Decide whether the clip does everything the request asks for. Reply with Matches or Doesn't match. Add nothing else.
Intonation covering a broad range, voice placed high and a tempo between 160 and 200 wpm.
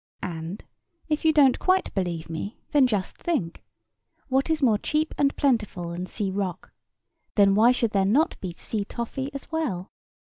Matches